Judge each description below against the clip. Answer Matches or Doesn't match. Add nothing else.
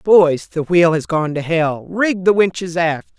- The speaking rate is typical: Matches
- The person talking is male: Doesn't match